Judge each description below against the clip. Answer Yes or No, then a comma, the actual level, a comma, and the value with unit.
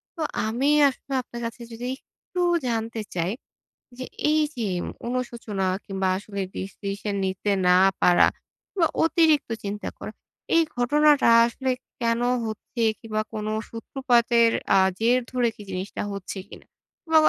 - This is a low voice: No, high, 230 Hz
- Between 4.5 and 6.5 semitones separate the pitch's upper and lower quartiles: No, average, 3.7 semitones